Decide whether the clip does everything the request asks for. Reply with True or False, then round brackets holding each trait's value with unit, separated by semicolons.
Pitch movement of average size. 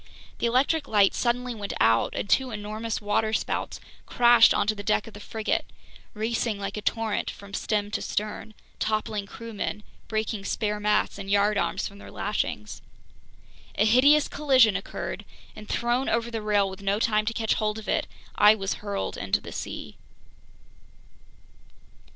False (2.0 semitones)